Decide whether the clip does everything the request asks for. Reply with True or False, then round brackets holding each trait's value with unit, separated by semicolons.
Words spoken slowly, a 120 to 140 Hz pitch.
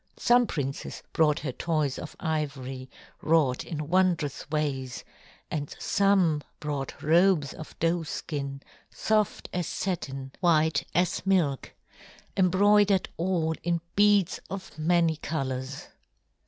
False (110 wpm; 160 Hz)